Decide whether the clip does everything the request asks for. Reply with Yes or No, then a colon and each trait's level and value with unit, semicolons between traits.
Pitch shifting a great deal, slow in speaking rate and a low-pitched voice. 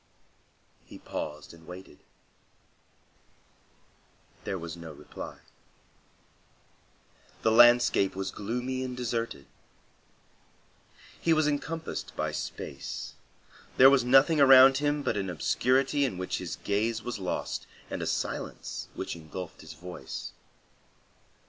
Yes: wide, 6.8 semitones; slow, 110 wpm; low, 115 Hz